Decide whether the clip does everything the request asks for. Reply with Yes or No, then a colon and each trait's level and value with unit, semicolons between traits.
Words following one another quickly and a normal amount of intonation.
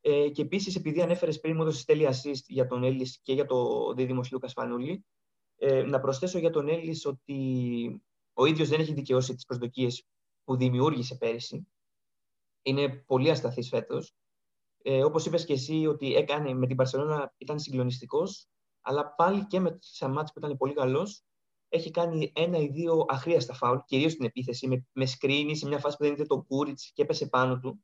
Yes: fast, 185 wpm; average, 3.5 semitones